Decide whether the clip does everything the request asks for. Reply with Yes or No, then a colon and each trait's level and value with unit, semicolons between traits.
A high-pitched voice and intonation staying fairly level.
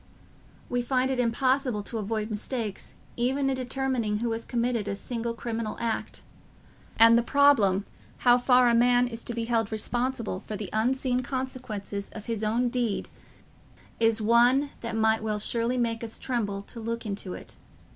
Yes: high, 230 Hz; narrow, 2.3 semitones